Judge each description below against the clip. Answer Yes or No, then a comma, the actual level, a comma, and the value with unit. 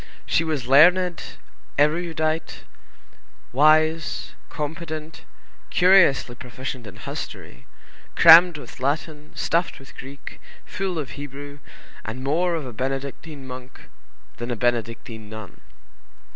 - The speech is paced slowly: Yes, slow, 105 wpm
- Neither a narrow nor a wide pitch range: Yes, average, 4.2 semitones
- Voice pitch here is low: No, medium, 145 Hz